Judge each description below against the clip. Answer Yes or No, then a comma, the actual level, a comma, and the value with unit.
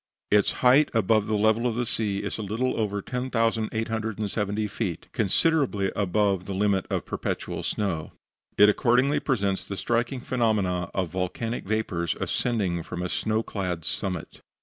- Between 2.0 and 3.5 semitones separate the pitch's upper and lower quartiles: Yes, average, 3.0 semitones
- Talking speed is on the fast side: No, average, 150 wpm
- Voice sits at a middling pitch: No, low, 105 Hz